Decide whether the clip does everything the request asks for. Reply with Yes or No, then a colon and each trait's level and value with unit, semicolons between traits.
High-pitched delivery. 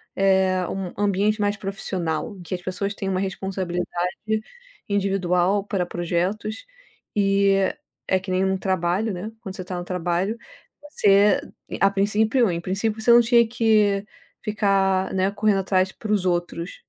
Yes: high, 195 Hz